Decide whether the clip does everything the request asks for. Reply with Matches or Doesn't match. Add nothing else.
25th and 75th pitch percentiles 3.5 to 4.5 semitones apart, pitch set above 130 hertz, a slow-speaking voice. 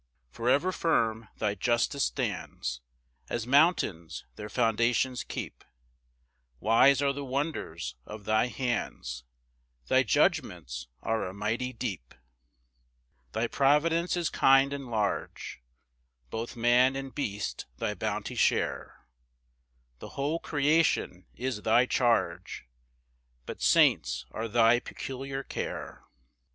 Doesn't match